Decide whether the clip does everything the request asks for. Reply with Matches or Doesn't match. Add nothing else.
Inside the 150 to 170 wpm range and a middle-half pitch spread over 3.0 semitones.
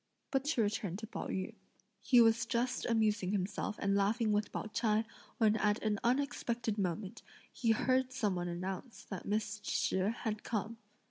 Doesn't match